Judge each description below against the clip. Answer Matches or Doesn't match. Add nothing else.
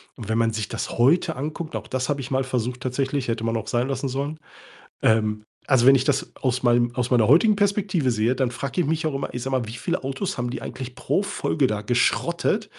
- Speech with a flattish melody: Doesn't match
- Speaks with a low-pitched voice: Matches